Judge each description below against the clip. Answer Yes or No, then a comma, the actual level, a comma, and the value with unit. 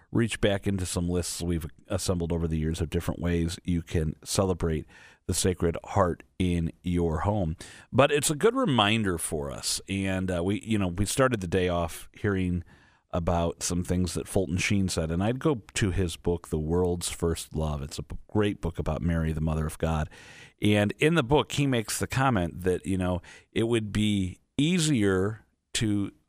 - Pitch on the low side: Yes, very low, 90 Hz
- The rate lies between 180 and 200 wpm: Yes, average, 190 wpm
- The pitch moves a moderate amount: Yes, average, 3.6 semitones